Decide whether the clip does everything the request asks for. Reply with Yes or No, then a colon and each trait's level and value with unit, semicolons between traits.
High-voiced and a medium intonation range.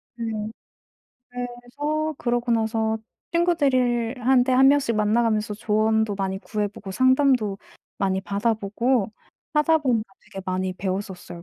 Yes: high, 225 Hz; average, 4.0 semitones